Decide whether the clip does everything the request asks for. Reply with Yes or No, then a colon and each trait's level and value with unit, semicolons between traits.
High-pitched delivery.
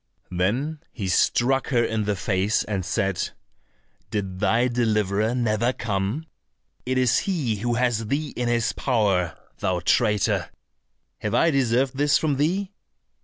No: low, 115 Hz